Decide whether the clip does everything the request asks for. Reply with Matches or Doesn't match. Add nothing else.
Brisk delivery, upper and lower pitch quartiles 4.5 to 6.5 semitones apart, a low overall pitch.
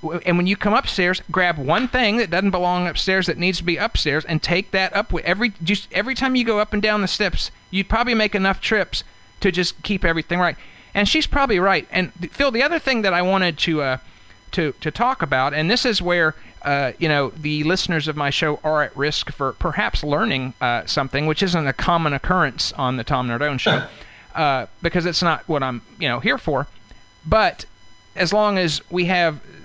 Doesn't match